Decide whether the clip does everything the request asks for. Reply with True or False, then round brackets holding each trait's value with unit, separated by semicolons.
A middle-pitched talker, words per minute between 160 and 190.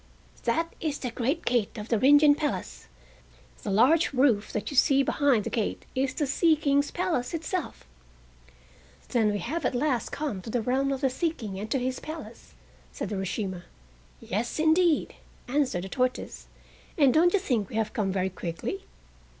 False (255 Hz; 180 wpm)